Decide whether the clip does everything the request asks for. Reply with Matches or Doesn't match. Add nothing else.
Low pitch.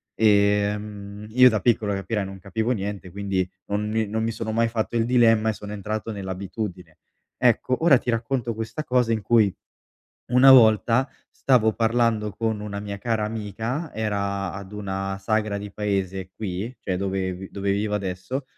Matches